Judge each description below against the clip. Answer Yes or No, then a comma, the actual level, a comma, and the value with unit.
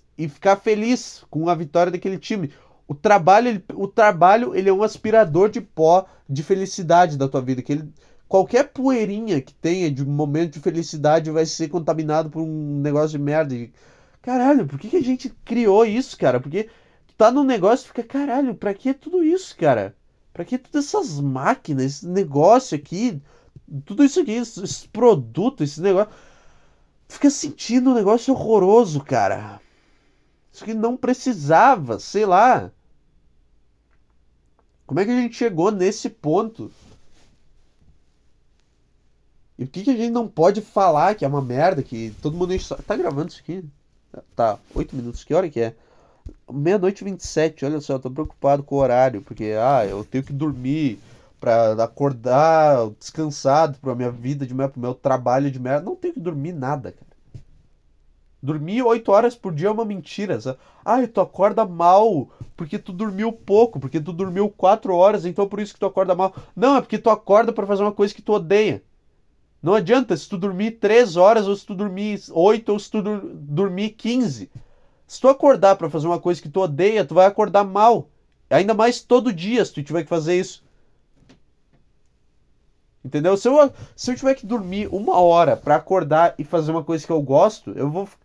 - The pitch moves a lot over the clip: Yes, wide, 7.0 semitones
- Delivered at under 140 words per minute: No, average, 180 wpm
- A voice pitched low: No, medium, 180 Hz